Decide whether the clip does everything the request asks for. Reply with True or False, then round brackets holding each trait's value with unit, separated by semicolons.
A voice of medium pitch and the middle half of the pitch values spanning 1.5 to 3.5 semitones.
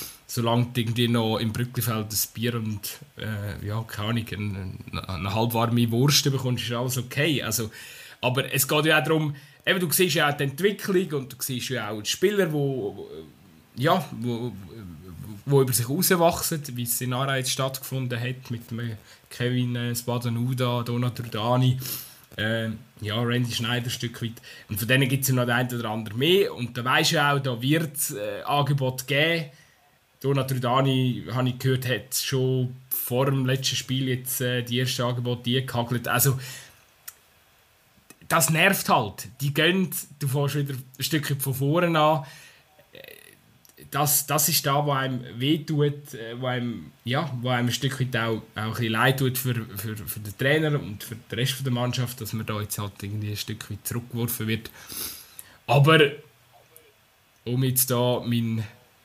False (125 Hz; 3.0 semitones)